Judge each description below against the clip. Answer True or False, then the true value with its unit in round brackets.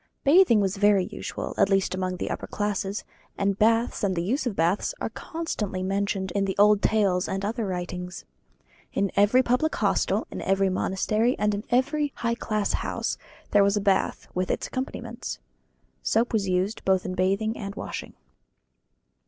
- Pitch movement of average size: True (3.0 semitones)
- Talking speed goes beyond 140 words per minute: True (170 wpm)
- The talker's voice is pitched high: True (200 Hz)